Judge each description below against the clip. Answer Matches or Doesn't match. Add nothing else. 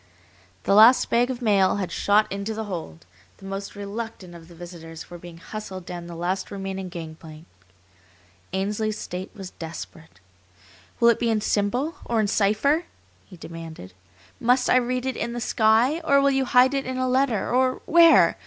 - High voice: Matches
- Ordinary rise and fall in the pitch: Doesn't match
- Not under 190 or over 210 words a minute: Doesn't match